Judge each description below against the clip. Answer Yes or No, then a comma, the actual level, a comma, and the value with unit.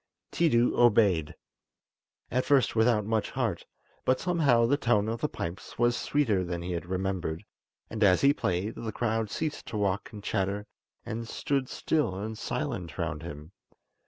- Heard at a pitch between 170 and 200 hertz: No, low, 110 Hz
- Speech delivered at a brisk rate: No, average, 160 wpm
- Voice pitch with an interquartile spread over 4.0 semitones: Yes, average, 4.5 semitones